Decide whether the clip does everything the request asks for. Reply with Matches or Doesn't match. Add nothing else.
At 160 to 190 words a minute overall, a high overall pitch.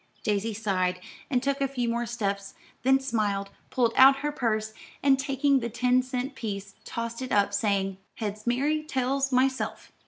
Matches